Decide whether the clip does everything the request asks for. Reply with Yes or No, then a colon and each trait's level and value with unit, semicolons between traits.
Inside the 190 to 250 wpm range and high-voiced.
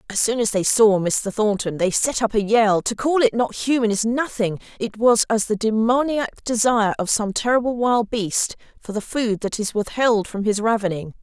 Yes: average, 200 wpm; high, 220 Hz